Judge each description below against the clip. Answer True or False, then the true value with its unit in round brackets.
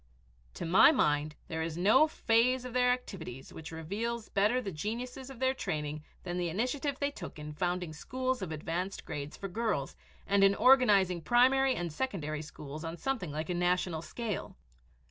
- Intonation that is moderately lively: False (7.5 semitones)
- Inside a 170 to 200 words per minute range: True (175 wpm)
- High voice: True (195 Hz)